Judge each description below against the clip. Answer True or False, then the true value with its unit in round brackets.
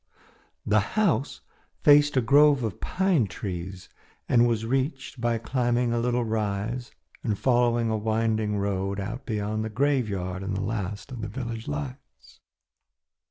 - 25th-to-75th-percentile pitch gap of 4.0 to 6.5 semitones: False (3.4 semitones)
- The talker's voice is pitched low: True (115 Hz)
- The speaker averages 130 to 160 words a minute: True (145 wpm)